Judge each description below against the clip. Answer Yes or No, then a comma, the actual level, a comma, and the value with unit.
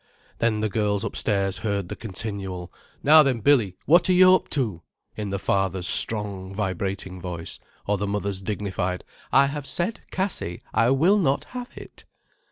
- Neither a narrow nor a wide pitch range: No, wide, 6.1 semitones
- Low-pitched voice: Yes, low, 105 Hz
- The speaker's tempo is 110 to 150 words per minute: No, average, 165 wpm